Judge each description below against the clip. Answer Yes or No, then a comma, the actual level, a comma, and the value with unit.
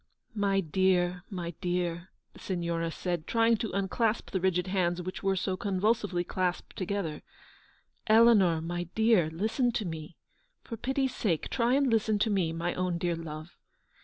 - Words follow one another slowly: No, average, 170 wpm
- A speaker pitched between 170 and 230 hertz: Yes, medium, 185 Hz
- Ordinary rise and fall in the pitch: Yes, average, 3.8 semitones